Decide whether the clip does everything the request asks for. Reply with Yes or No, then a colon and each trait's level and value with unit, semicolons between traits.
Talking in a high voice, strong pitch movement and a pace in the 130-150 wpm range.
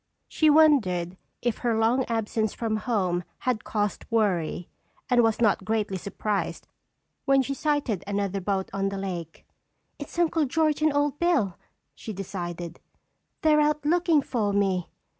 Yes: high, 220 Hz; wide, 6.7 semitones; average, 145 wpm